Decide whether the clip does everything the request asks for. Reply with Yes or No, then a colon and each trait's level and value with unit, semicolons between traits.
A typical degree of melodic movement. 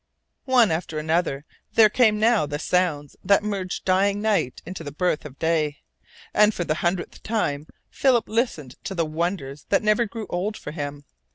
No: wide, 5.7 semitones